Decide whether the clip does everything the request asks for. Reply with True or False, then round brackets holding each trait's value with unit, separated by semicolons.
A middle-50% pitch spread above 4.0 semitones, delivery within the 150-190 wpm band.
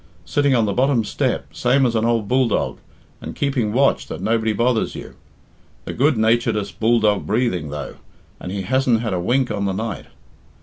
False (3.3 semitones; 180 wpm)